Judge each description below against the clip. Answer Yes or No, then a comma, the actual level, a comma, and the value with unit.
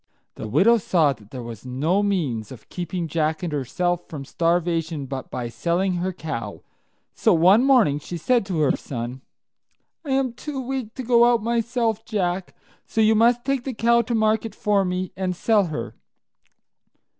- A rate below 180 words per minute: Yes, average, 170 wpm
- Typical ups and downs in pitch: No, wide, 6.8 semitones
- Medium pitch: Yes, medium, 180 Hz